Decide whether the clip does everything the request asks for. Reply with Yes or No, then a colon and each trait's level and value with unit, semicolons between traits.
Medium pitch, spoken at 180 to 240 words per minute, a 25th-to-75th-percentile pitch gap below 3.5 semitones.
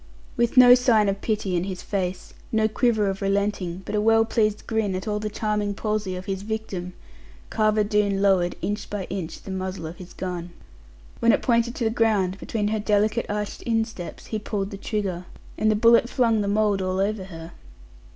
No: high, 210 Hz; average, 200 wpm; narrow, 2.5 semitones